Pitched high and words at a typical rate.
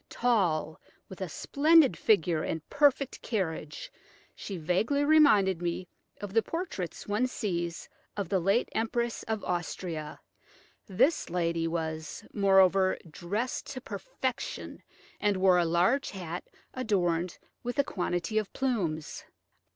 No: high, 195 Hz; slow, 125 wpm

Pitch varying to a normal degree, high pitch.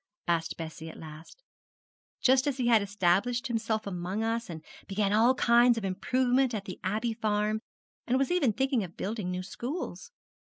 Yes: average, 4.7 semitones; high, 220 Hz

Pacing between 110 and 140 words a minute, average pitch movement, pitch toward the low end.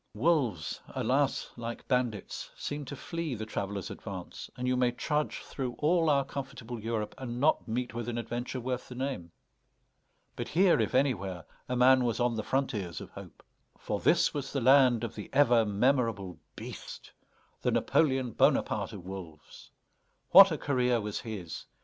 No: average, 165 wpm; average, 3.7 semitones; low, 125 Hz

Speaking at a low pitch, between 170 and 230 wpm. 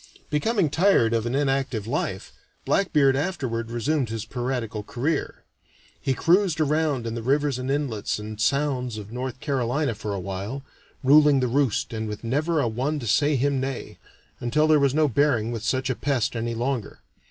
Yes: low, 130 Hz; average, 175 wpm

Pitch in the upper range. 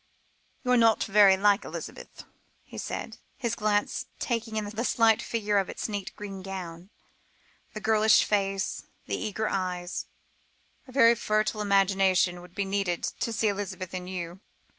Yes: high, 205 Hz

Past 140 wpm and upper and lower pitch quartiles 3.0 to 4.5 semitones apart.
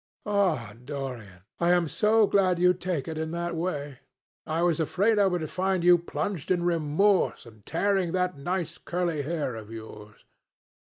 Yes: average, 165 wpm; average, 4.0 semitones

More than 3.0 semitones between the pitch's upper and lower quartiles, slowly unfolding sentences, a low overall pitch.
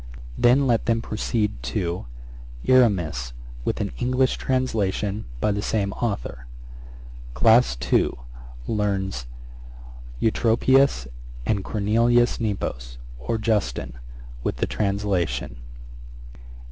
Yes: wide, 5.5 semitones; slow, 95 wpm; low, 105 Hz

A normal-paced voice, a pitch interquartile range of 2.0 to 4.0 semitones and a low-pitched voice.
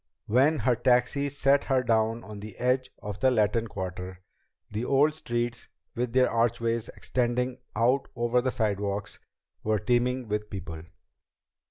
Yes: average, 145 wpm; average, 3.2 semitones; low, 120 Hz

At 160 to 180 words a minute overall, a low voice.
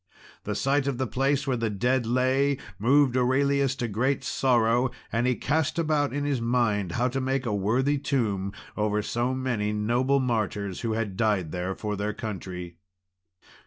Yes: average, 170 wpm; low, 120 Hz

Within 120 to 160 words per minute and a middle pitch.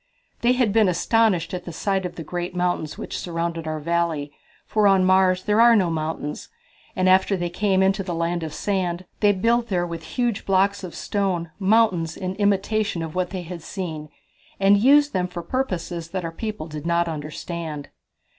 No: average, 190 wpm; medium, 180 Hz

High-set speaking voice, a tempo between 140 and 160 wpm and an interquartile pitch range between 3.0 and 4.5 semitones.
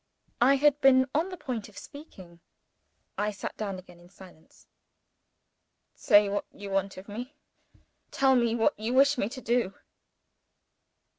No: high, 225 Hz; average, 150 wpm; wide, 5.4 semitones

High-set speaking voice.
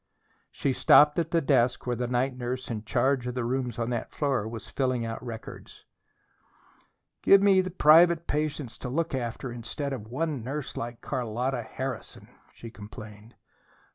No: low, 125 Hz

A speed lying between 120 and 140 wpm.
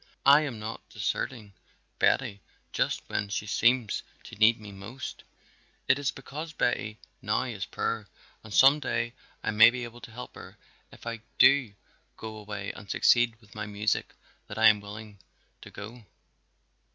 No: average, 165 wpm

